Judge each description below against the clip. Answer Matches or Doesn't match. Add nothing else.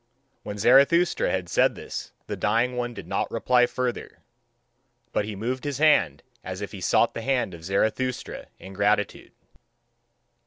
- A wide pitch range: Doesn't match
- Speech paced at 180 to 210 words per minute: Doesn't match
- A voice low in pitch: Matches